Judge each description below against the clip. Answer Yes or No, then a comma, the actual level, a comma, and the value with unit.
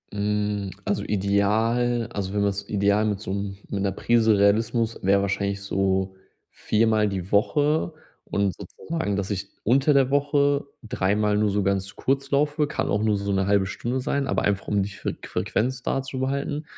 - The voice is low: Yes, low, 105 Hz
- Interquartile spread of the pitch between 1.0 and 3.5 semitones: No, average, 4.2 semitones